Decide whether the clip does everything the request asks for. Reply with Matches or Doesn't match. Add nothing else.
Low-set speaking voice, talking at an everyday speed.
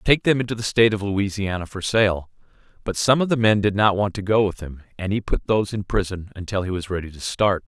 Doesn't match